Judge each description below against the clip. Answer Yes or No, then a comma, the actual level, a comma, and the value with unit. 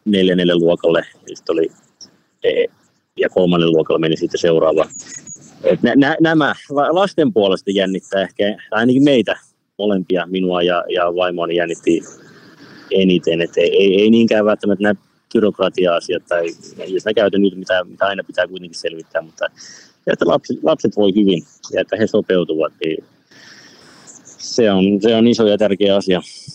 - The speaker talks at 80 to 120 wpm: No, average, 140 wpm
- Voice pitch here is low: Yes, very low, 95 Hz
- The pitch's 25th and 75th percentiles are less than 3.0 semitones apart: No, average, 3.3 semitones